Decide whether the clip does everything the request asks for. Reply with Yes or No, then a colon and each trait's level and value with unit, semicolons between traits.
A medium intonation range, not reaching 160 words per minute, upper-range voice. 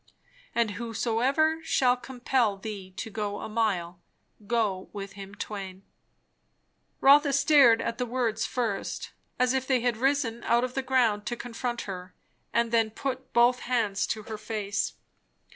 Yes: average, 3.3 semitones; average, 150 wpm; high, 230 Hz